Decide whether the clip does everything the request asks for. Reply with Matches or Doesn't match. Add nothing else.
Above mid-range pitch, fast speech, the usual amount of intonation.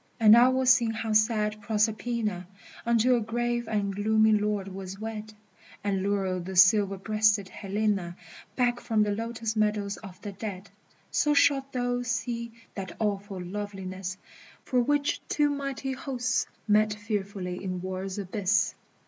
Doesn't match